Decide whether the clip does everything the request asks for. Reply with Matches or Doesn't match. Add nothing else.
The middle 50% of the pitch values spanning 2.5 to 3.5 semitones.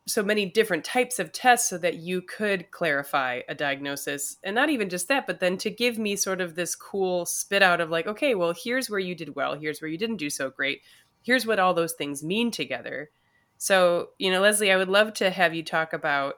Doesn't match